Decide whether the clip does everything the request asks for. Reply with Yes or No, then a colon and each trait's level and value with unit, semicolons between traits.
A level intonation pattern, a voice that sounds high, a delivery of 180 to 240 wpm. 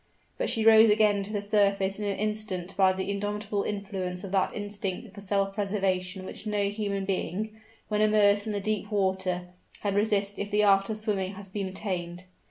Yes: narrow, 1.6 semitones; high, 200 Hz; average, 190 wpm